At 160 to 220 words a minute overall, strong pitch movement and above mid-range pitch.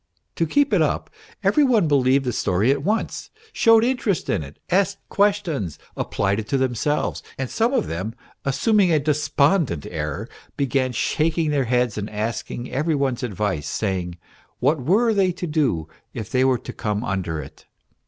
No: average, 170 wpm; wide, 8.0 semitones; low, 135 Hz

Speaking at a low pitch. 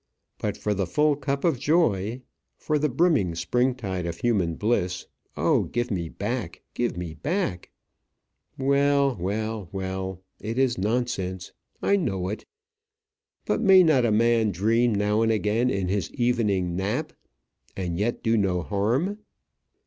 Yes: low, 110 Hz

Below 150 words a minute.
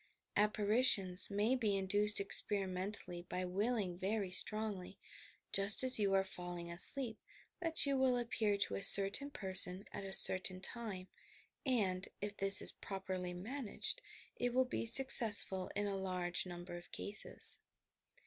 Yes: average, 140 wpm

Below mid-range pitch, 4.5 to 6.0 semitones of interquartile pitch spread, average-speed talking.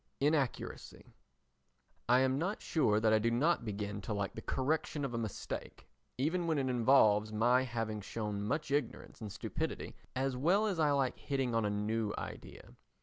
Yes: low, 125 Hz; average, 4.9 semitones; average, 175 wpm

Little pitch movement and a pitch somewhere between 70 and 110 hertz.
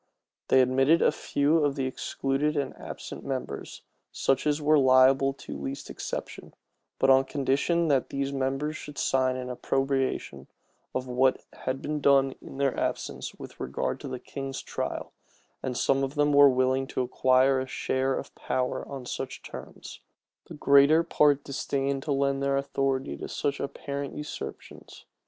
No: narrow, 1.3 semitones; low, 135 Hz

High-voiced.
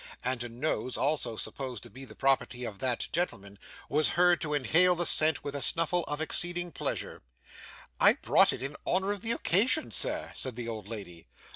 No: medium, 140 Hz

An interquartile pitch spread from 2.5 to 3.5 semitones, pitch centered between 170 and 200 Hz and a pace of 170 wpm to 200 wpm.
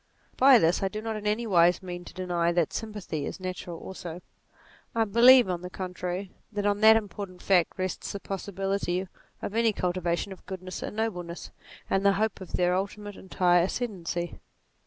Yes: average, 2.8 semitones; high, 190 Hz; average, 180 wpm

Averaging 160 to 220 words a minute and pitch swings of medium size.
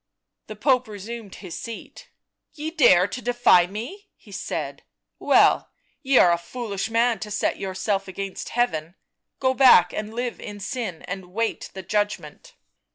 Yes: average, 165 wpm; average, 4.3 semitones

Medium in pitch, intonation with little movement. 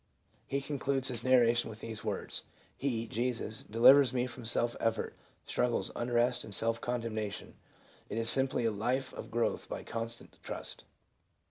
No: low, 120 Hz; narrow, 2.0 semitones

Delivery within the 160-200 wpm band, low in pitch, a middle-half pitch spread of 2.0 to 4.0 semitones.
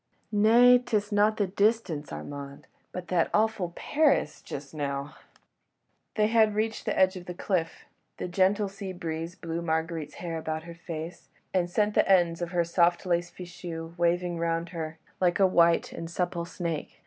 No: average, 170 wpm; medium, 175 Hz; average, 3.2 semitones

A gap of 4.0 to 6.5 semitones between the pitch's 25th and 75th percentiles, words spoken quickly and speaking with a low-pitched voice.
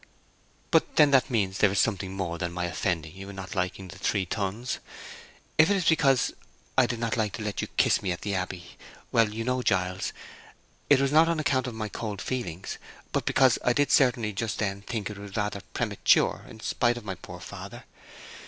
Yes: average, 4.5 semitones; fast, 210 wpm; low, 105 Hz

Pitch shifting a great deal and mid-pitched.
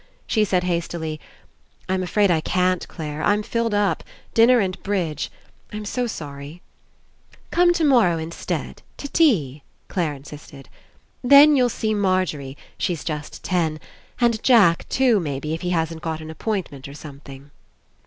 Yes: wide, 5.9 semitones; medium, 180 Hz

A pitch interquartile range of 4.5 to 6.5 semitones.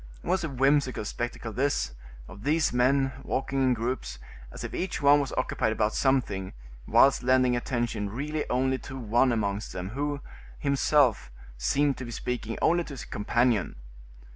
No: average, 3.8 semitones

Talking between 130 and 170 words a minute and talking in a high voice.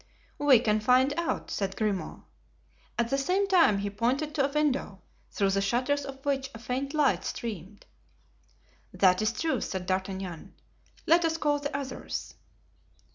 Yes: average, 155 wpm; very high, 255 Hz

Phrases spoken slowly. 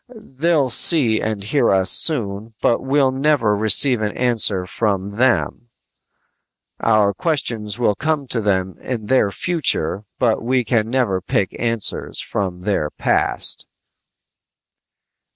Yes: slow, 125 wpm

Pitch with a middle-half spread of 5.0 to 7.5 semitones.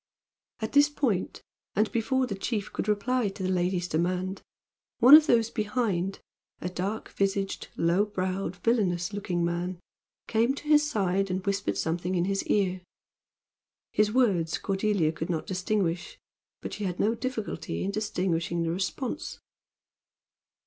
No: average, 3.5 semitones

